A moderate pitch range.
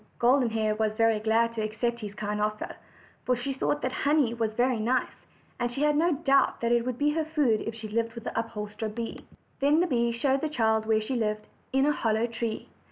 Yes: average, 3.5 semitones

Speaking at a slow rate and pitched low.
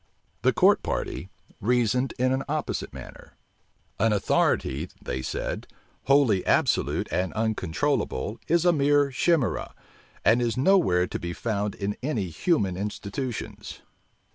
Yes: slow, 125 wpm; low, 115 Hz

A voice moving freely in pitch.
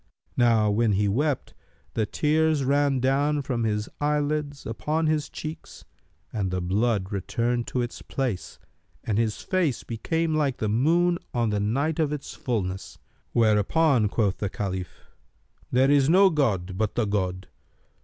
Yes: wide, 6.1 semitones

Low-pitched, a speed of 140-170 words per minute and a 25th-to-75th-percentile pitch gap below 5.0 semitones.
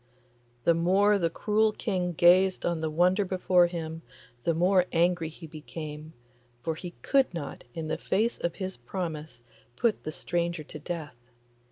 No: medium, 170 Hz; average, 160 wpm; average, 2.7 semitones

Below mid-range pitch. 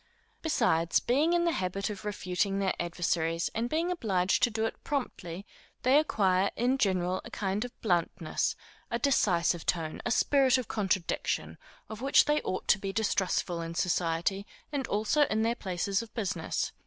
No: high, 200 Hz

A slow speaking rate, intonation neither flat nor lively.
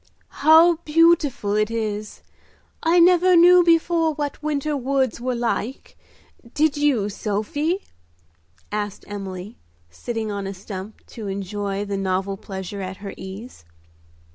No: slow, 125 wpm; wide, 7.4 semitones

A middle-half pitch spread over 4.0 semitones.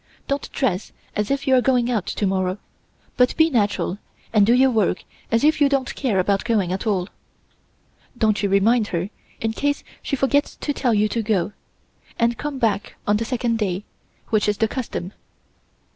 Yes: average, 4.4 semitones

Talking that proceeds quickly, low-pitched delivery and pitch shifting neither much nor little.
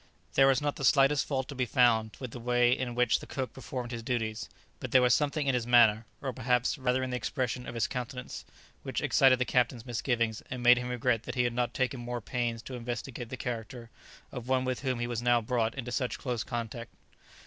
No: fast, 230 wpm; low, 125 Hz; narrow, 1.6 semitones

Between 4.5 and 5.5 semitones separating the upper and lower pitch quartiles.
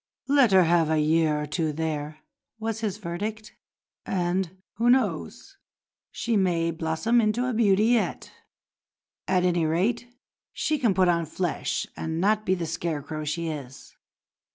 Yes: average, 5.1 semitones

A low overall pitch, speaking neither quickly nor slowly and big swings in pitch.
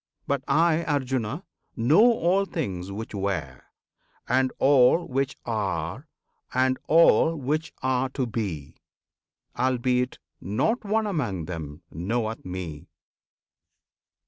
No: low, 125 Hz; slow, 105 wpm; wide, 7.5 semitones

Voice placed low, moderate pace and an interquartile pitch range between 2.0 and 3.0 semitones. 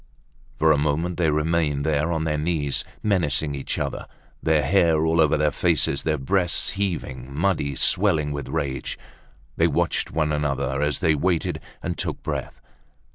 Yes: very low, 75 Hz; average, 160 wpm; narrow, 2.5 semitones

